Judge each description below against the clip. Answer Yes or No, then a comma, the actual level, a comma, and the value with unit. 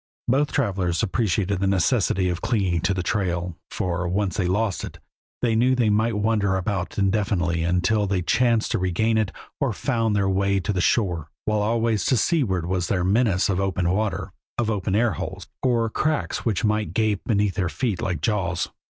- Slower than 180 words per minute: No, average, 185 wpm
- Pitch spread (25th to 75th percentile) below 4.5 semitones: Yes, average, 3.5 semitones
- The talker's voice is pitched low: Yes, low, 100 Hz